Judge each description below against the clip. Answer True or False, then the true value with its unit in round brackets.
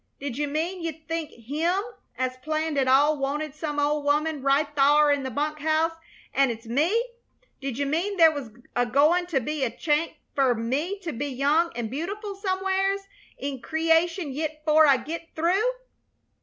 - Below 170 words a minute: False (175 wpm)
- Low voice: False (300 Hz)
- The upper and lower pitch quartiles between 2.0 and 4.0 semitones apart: True (3.1 semitones)